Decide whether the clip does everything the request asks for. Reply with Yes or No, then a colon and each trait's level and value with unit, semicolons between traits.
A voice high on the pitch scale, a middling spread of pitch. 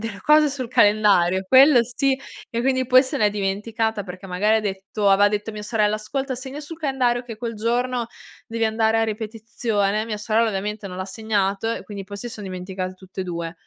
Yes: high, 215 Hz; average, 3.2 semitones